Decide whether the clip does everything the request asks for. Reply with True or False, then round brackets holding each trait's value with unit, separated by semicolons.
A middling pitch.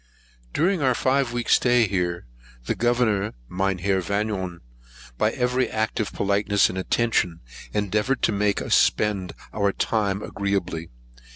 False (105 Hz)